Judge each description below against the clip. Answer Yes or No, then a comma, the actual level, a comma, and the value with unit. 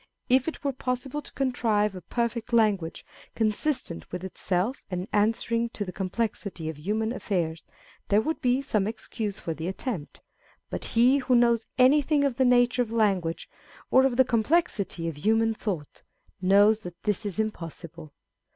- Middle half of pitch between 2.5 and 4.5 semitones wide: No, average, 5.1 semitones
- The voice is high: Yes, high, 220 Hz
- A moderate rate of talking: Yes, average, 165 wpm